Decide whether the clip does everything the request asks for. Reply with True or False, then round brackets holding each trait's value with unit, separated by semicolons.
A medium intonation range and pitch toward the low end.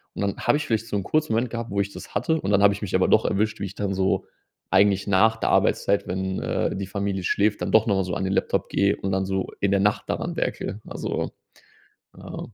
False (1.9 semitones; 100 Hz)